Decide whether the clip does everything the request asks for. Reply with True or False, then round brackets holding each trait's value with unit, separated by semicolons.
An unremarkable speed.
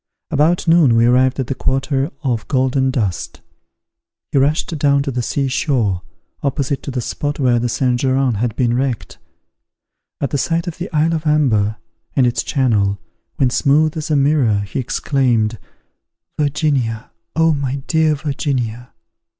True (160 wpm)